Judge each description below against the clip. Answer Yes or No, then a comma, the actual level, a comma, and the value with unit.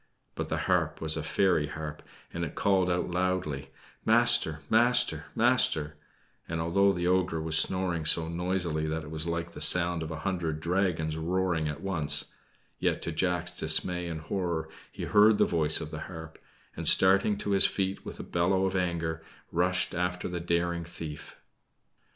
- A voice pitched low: Yes, very low, 85 Hz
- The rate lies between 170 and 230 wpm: Yes, average, 175 wpm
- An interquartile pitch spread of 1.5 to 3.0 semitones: Yes, average, 2.7 semitones